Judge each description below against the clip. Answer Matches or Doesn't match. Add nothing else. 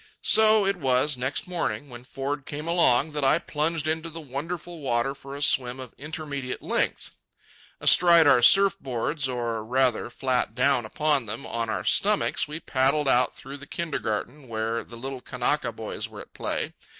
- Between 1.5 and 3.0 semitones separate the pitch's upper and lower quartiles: Doesn't match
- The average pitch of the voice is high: Doesn't match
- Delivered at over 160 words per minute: Matches